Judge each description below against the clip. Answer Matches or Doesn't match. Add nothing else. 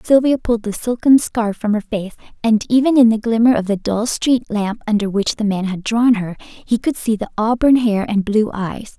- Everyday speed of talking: Doesn't match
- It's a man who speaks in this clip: Doesn't match